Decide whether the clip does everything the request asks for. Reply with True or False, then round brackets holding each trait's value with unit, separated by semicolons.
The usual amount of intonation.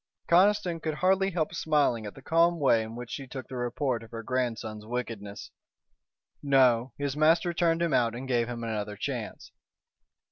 False (6.0 semitones)